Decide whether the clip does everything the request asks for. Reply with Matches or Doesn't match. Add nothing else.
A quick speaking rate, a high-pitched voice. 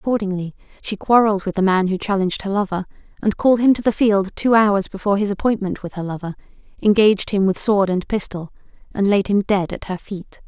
Matches